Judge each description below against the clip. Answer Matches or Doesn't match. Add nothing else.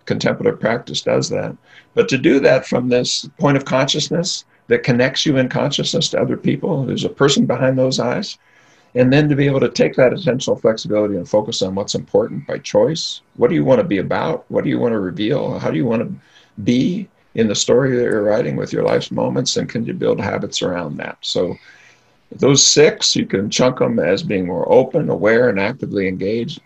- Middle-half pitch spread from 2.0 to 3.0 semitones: Doesn't match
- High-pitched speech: Doesn't match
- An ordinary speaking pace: Doesn't match